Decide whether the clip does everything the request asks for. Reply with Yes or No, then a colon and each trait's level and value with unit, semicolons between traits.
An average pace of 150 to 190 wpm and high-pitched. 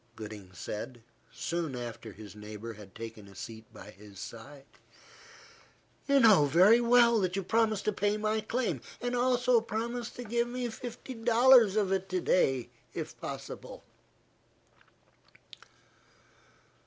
No: slow, 135 wpm; high, 195 Hz